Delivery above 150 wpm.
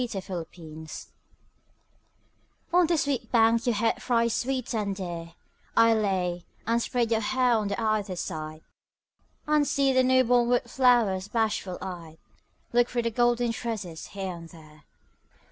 No: average, 145 wpm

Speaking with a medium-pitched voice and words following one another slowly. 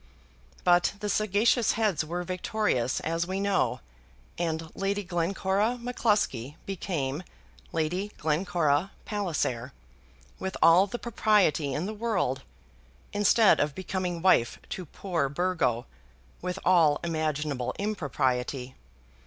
Yes: medium, 175 Hz; slow, 110 wpm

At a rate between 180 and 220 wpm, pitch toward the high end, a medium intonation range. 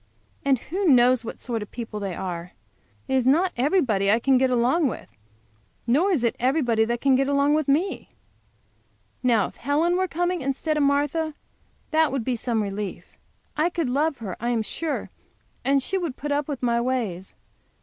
Yes: average, 185 wpm; very high, 265 Hz; average, 4.6 semitones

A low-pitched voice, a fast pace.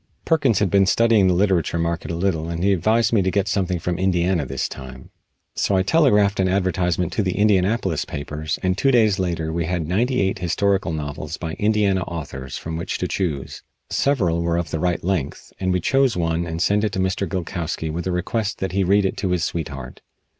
Yes: very low, 90 Hz; fast, 210 wpm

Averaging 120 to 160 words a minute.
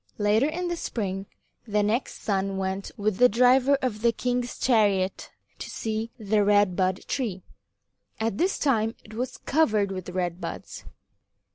Yes: average, 155 wpm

